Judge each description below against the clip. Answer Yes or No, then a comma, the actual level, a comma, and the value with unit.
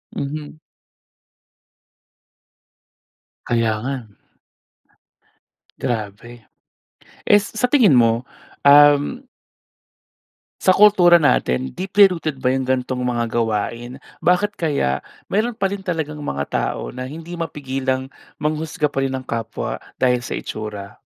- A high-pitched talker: No, low, 135 Hz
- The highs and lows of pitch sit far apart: Yes, wide, 6.0 semitones